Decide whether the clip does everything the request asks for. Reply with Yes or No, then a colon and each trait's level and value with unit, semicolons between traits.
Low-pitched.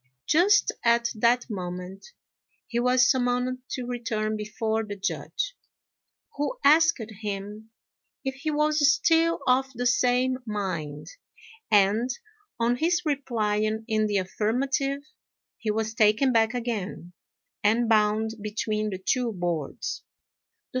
No: high, 230 Hz